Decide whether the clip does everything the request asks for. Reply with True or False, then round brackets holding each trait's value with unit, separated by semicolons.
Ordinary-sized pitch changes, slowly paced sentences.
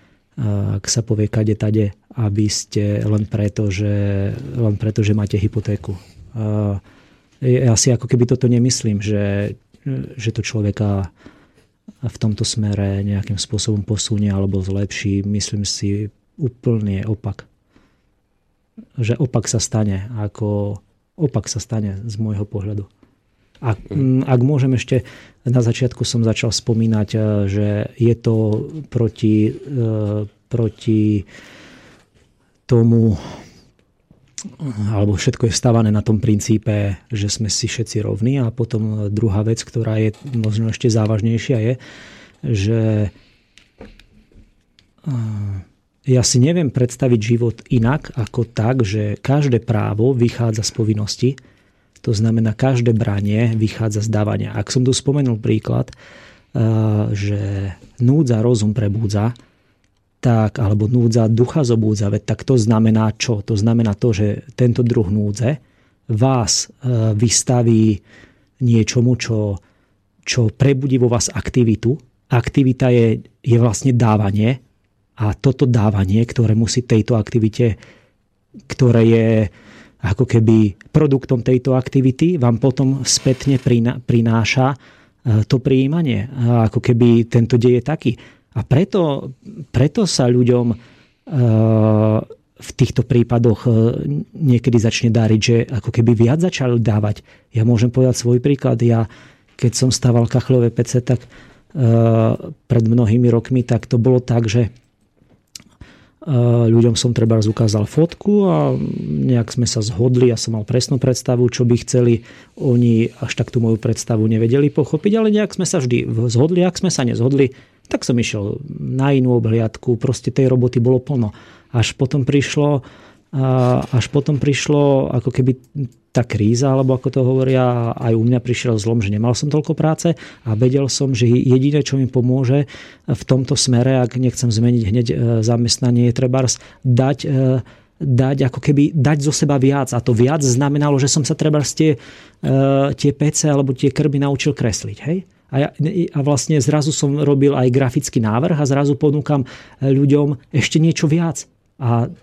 False (3.3 semitones; 135 wpm)